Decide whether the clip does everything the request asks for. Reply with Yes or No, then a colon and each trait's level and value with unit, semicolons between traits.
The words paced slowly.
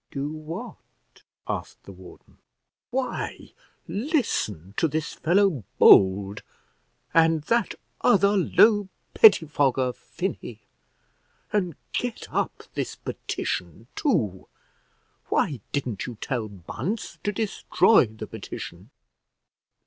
Yes: slow, 95 wpm